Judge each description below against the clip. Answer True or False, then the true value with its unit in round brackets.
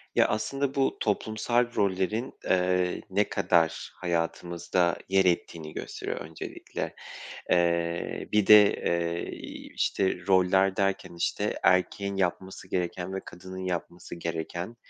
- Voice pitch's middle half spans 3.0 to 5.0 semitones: False (2.4 semitones)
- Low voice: True (90 Hz)